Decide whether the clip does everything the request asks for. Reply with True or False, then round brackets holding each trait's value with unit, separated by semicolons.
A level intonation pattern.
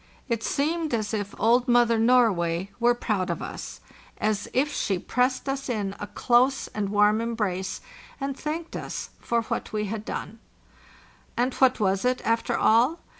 False (3.5 semitones)